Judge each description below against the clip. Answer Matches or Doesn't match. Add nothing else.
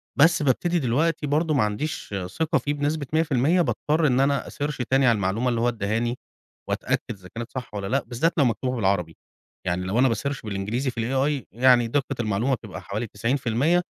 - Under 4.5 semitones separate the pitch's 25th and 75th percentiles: Doesn't match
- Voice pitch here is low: Matches